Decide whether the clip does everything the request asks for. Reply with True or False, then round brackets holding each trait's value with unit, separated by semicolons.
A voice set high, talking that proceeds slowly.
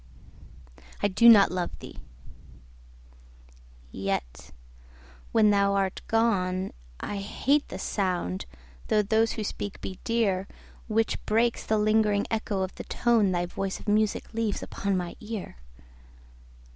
True (195 Hz; 130 wpm)